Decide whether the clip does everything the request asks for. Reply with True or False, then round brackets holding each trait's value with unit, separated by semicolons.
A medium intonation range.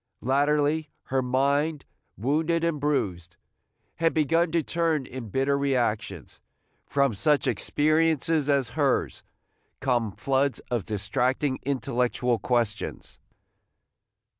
True (3.6 semitones)